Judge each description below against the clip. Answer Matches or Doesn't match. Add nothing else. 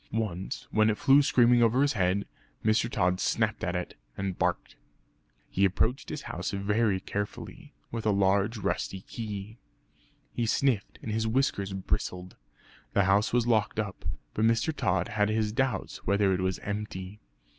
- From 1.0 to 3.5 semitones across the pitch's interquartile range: Matches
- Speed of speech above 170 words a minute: Doesn't match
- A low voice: Matches